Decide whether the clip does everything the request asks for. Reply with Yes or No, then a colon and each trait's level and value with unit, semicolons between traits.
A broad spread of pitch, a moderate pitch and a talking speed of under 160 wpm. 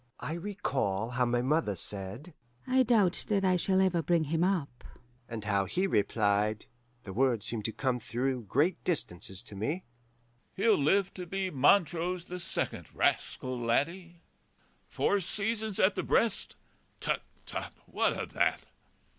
Yes: wide, 8.2 semitones; medium, 155 Hz; average, 150 wpm